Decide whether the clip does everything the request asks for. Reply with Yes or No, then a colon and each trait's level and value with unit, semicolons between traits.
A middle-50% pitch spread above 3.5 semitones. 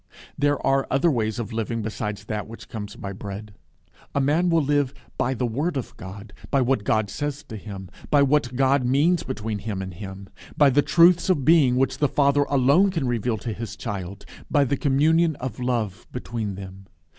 Yes: average, 5.2 semitones